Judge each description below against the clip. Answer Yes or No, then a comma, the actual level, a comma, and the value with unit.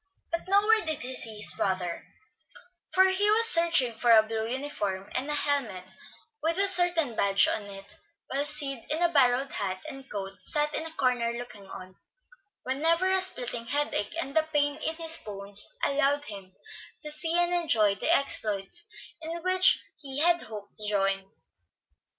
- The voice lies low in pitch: No, very high, 275 Hz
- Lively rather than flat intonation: Yes, wide, 7.7 semitones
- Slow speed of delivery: No, average, 170 wpm